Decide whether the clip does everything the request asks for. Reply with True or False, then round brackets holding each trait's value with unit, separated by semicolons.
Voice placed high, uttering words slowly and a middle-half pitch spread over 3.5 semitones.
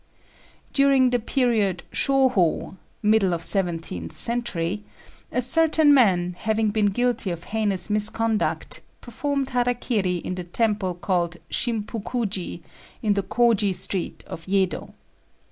True (210 Hz; 120 wpm; 4.8 semitones)